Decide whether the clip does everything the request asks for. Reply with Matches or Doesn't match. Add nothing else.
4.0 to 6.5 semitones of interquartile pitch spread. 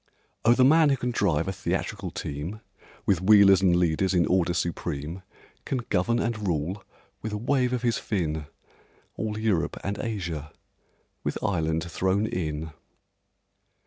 Matches